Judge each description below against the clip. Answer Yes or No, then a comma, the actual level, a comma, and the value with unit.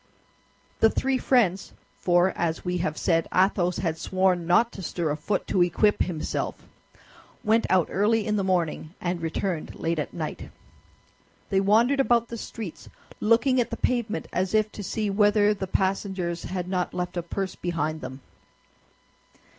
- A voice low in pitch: No, high, 190 Hz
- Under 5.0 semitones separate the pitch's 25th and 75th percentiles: Yes, average, 3.4 semitones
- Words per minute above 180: No, average, 155 wpm